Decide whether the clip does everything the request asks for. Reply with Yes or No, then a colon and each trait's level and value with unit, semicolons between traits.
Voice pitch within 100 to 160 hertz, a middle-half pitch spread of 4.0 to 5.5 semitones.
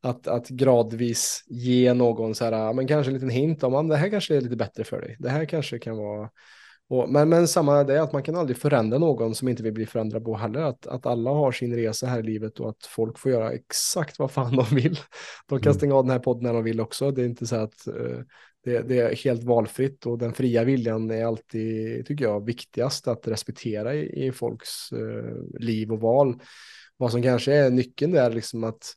No: low, 125 Hz; average, 3.1 semitones